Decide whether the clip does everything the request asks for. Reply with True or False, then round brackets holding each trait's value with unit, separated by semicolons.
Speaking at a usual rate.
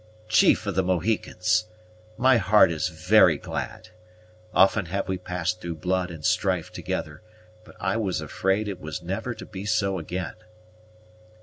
True (150 wpm)